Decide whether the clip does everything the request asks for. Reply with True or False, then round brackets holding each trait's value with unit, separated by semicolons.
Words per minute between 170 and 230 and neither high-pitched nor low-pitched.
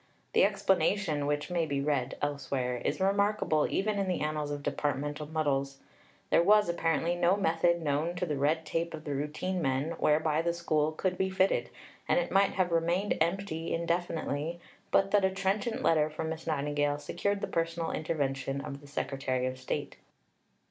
True (175 wpm; 160 Hz)